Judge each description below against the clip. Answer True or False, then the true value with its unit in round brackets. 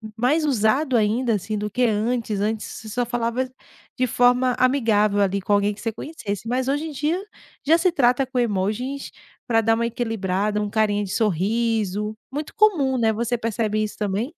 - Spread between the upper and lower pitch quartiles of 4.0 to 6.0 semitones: False (3.4 semitones)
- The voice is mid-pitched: False (225 Hz)